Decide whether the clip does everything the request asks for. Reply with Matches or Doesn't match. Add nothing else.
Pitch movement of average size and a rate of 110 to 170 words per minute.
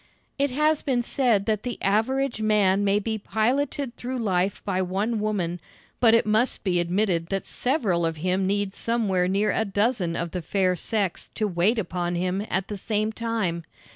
Doesn't match